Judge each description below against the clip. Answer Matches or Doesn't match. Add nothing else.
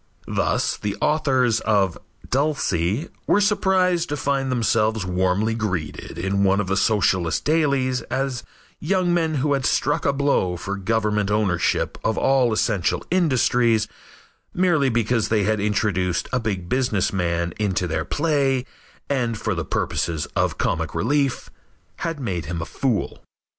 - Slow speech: Doesn't match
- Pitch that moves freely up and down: Matches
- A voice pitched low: Matches